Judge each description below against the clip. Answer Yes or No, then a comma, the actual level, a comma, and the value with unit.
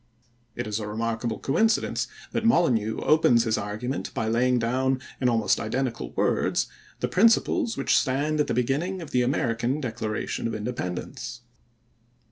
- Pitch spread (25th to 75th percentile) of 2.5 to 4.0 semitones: Yes, average, 3.5 semitones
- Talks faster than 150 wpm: No, average, 145 wpm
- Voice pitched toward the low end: Yes, low, 125 Hz